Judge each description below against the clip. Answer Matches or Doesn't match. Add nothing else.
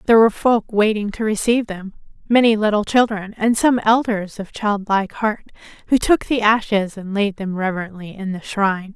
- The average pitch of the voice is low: Doesn't match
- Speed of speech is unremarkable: Matches